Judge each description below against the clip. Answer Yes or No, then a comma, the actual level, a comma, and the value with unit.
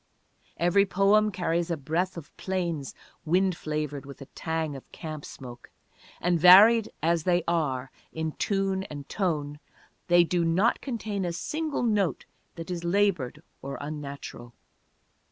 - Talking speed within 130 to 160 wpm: Yes, average, 140 wpm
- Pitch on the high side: No, medium, 170 Hz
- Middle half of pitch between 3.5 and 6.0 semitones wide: Yes, average, 4.0 semitones